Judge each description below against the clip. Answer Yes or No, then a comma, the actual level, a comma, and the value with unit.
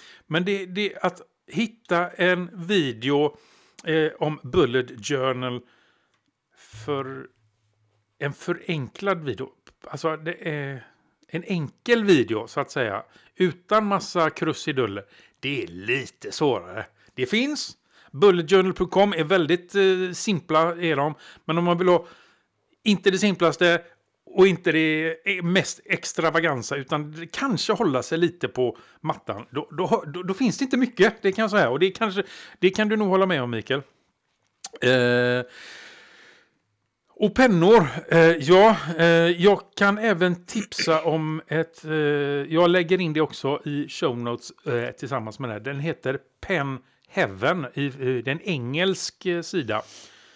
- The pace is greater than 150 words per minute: No, average, 140 wpm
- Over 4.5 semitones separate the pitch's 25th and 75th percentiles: Yes, average, 5.3 semitones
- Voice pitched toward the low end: No, medium, 165 Hz